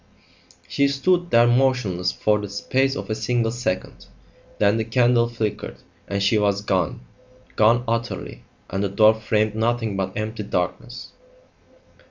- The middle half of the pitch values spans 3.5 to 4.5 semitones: No, average, 2.9 semitones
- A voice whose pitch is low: Yes, low, 110 Hz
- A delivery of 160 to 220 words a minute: No, average, 145 wpm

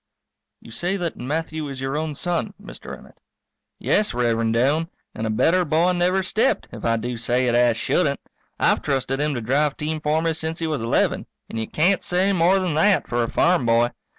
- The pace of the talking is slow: No, fast, 205 wpm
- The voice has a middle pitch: Yes, medium, 150 Hz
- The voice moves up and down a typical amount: No, wide, 6.2 semitones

